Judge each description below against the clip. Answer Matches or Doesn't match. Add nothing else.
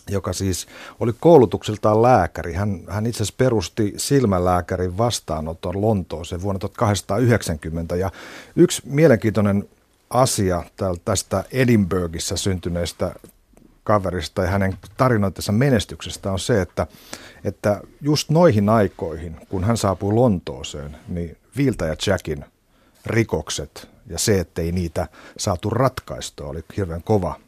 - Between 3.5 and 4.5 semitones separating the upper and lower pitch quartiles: Matches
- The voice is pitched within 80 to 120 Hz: Matches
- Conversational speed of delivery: Matches